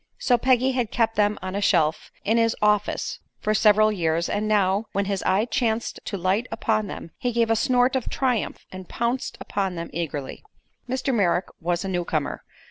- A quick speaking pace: No, average, 190 wpm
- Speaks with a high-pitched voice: Yes, high, 210 Hz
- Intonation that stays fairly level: No, average, 3.9 semitones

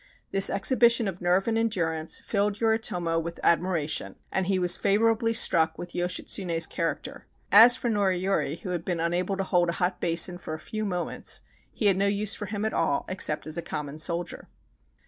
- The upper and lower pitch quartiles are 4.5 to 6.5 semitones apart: No, average, 3.4 semitones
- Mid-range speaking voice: Yes, medium, 180 Hz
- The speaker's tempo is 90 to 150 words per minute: No, average, 185 wpm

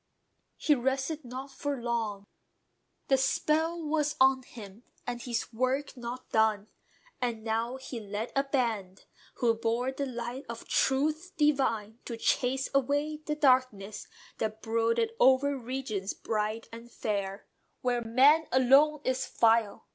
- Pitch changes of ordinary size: Yes, average, 3.4 semitones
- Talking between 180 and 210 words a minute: No, slow, 135 wpm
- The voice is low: No, very high, 250 Hz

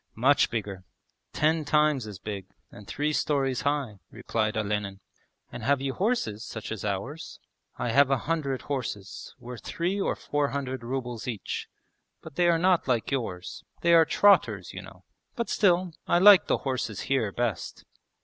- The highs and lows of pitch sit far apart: Yes, wide, 5.8 semitones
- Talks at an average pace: Yes, average, 165 wpm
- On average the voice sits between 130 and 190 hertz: Yes, low, 135 Hz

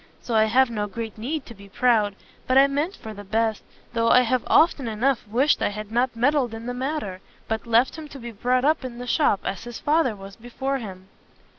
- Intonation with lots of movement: No, average, 3.5 semitones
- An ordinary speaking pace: No, fast, 230 wpm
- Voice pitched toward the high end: Yes, high, 235 Hz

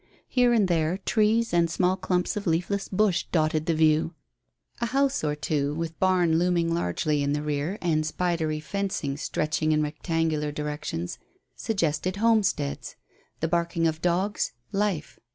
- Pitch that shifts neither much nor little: Yes, average, 3.6 semitones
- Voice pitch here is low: No, medium, 165 Hz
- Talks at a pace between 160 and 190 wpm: No, average, 150 wpm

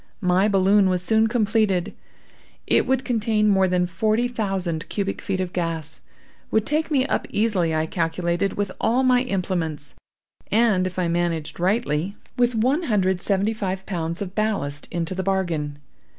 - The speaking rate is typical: Yes, average, 165 wpm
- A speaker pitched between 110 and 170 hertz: No, high, 190 Hz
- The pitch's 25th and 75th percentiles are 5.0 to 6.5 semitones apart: No, average, 4.0 semitones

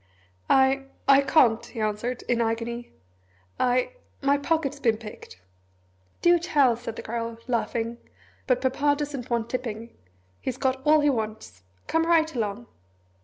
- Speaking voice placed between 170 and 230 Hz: No, high, 245 Hz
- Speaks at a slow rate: No, average, 150 wpm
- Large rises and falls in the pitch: No, average, 3.5 semitones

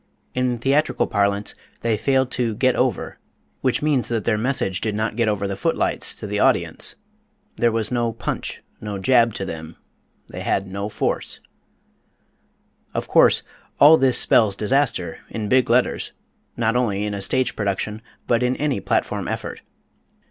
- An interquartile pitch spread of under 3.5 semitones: No, average, 3.8 semitones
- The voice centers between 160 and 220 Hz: No, low, 115 Hz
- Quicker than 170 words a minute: No, average, 165 wpm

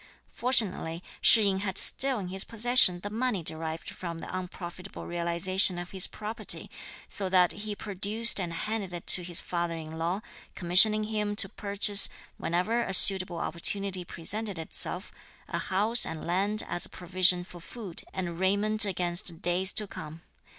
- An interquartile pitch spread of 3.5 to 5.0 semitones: No, average, 3.1 semitones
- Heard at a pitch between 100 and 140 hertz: No, medium, 185 Hz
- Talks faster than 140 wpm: Yes, average, 160 wpm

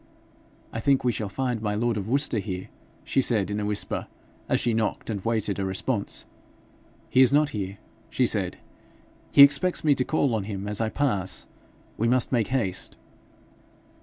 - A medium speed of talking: Yes, average, 180 wpm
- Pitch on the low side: Yes, low, 110 Hz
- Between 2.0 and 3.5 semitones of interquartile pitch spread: No, average, 4.2 semitones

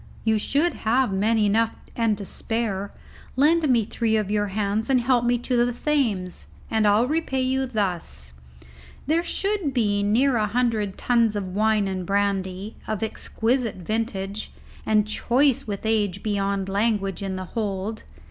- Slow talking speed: No, average, 155 wpm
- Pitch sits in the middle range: No, high, 220 Hz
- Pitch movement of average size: Yes, average, 3.3 semitones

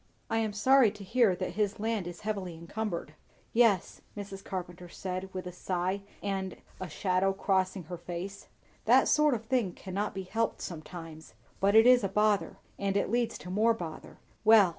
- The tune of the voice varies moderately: Yes, average, 3.2 semitones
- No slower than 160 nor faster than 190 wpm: Yes, average, 180 wpm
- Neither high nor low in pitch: No, high, 195 Hz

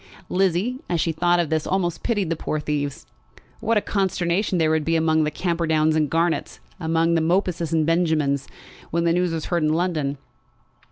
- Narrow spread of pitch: Yes, narrow, 1.9 semitones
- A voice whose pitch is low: No, medium, 165 Hz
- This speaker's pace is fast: No, average, 185 wpm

